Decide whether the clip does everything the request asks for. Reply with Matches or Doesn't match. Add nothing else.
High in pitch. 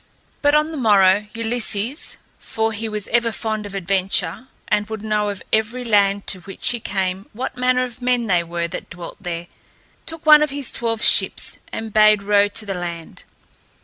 Matches